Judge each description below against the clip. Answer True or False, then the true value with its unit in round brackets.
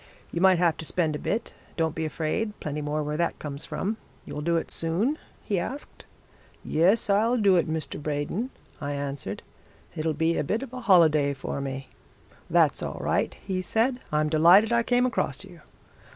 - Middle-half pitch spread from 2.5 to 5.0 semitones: False (5.4 semitones)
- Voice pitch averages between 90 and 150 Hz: False (165 Hz)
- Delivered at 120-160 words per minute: False (185 wpm)